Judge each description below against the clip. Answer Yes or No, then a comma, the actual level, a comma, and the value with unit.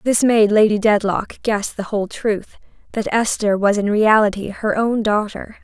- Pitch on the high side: Yes, high, 210 Hz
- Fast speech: No, average, 160 wpm